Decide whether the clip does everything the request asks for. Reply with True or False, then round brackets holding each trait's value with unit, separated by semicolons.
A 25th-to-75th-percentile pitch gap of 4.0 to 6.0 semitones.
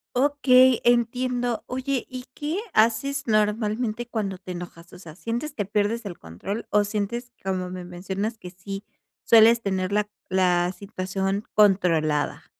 True (4.3 semitones)